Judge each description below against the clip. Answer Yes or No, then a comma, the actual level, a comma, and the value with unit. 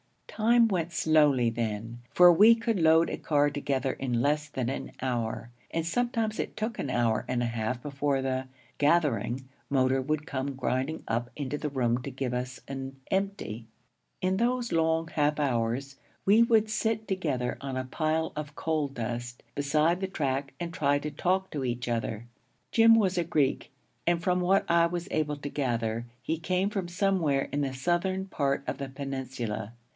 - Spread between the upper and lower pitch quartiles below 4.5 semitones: No, average, 5.1 semitones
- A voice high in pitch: No, medium, 145 Hz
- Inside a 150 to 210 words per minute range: Yes, average, 180 wpm